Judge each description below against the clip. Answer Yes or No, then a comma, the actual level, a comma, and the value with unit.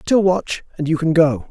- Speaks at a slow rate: No, fast, 240 wpm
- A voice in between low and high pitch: Yes, medium, 160 Hz